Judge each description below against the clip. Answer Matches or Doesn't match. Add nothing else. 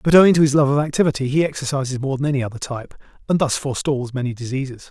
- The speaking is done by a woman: Doesn't match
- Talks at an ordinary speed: Doesn't match